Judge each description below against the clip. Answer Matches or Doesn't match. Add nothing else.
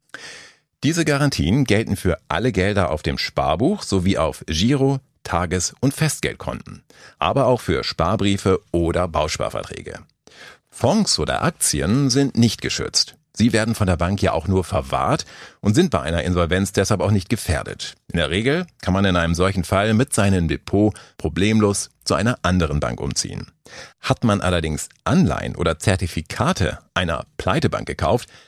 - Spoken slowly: Doesn't match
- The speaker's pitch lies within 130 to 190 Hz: Doesn't match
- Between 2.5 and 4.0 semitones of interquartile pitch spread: Doesn't match